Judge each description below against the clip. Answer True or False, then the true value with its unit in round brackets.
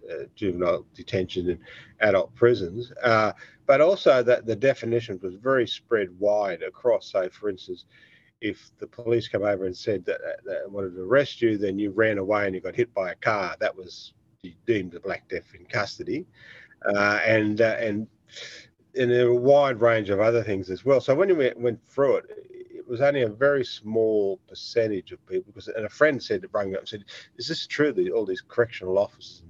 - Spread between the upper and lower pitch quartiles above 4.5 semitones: True (5.6 semitones)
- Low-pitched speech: True (120 Hz)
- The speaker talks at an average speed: False (210 wpm)